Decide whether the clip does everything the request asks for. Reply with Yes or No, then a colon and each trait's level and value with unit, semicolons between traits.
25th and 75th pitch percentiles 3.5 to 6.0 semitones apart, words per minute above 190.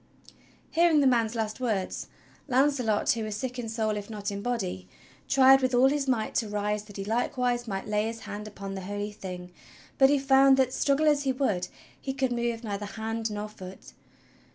Yes: average, 4.0 semitones; average, 200 wpm